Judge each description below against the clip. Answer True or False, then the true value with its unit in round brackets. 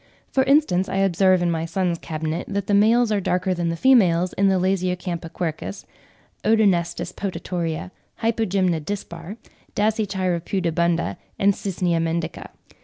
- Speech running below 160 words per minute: True (135 wpm)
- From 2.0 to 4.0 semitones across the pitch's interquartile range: True (2.9 semitones)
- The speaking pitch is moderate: True (180 Hz)